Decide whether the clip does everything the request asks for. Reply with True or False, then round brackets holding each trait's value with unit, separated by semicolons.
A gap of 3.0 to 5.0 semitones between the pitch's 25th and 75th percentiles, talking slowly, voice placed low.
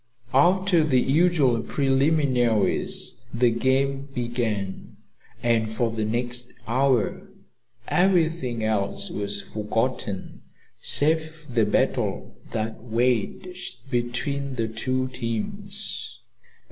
True (3.6 semitones; 90 wpm; 125 Hz)